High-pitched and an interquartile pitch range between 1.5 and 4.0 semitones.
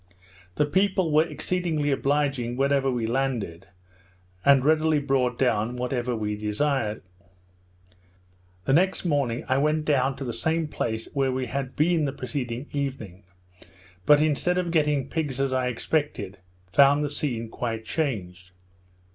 No: low, 135 Hz; average, 3.6 semitones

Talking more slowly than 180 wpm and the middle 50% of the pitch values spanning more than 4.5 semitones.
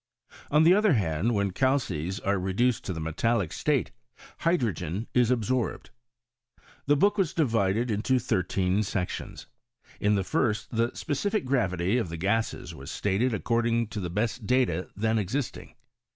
Yes: average, 155 wpm; average, 5.0 semitones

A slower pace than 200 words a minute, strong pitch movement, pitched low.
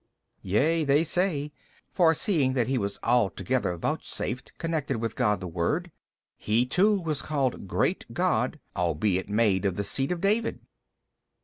Yes: average, 150 wpm; wide, 8.0 semitones; low, 130 Hz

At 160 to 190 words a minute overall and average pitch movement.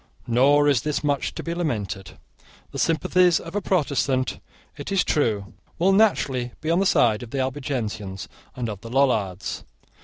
No: average, 165 wpm; wide, 6.0 semitones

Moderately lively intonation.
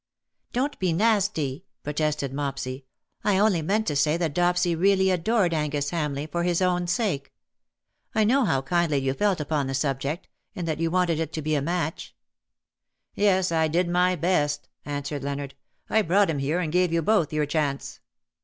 Yes: average, 3.9 semitones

